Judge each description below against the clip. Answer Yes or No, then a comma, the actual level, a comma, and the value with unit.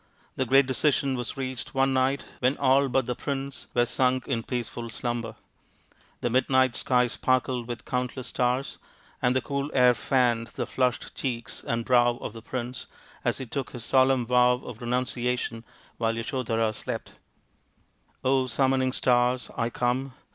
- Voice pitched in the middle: No, low, 125 Hz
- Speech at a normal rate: Yes, average, 155 wpm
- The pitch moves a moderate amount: No, narrow, 1.6 semitones